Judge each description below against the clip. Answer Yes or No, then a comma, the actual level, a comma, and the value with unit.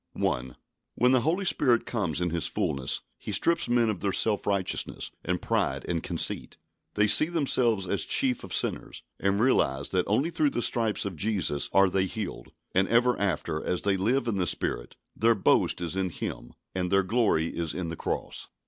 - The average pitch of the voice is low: Yes, low, 100 Hz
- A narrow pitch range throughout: No, average, 5.2 semitones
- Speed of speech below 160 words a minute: No, average, 195 wpm